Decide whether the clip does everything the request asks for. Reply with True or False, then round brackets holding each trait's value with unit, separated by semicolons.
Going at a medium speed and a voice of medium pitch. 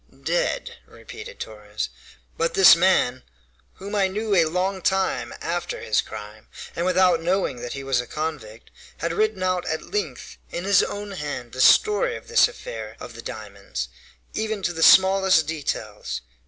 True (165 wpm; 180 Hz)